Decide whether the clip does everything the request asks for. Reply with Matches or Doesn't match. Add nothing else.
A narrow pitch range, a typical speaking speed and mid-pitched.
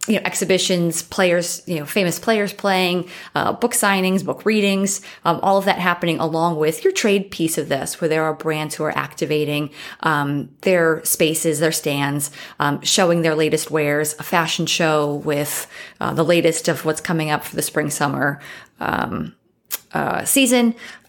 Doesn't match